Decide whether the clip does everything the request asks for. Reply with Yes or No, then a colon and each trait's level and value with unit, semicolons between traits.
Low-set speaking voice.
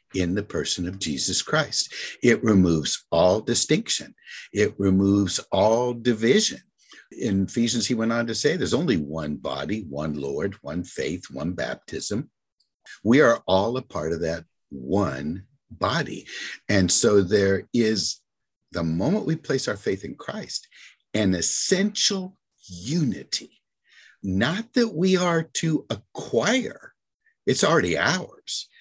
Yes: low, 110 Hz